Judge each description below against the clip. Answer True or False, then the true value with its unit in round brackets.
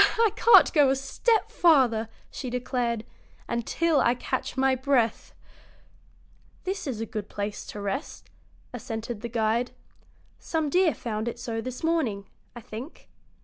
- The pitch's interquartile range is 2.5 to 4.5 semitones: True (4.2 semitones)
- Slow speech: False (145 wpm)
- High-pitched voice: True (245 Hz)